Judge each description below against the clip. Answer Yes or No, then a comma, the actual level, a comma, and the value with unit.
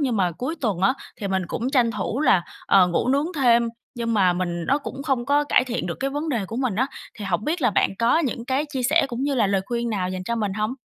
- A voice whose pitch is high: Yes, high, 235 Hz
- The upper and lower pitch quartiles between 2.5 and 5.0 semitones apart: No, wide, 5.4 semitones